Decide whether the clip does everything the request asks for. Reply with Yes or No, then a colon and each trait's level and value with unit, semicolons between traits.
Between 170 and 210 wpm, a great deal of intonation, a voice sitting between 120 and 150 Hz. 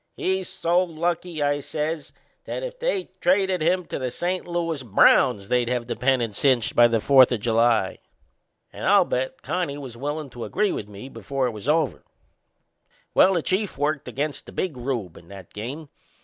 Yes: average, 185 wpm; wide, 6.2 semitones; medium, 140 Hz